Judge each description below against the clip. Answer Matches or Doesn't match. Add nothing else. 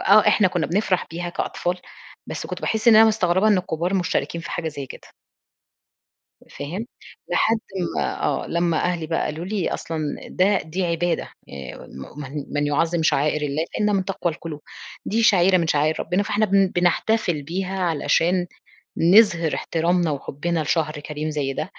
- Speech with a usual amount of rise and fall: Matches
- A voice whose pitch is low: Doesn't match